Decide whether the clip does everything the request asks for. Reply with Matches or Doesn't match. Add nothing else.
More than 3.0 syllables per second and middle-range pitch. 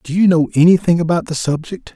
Matches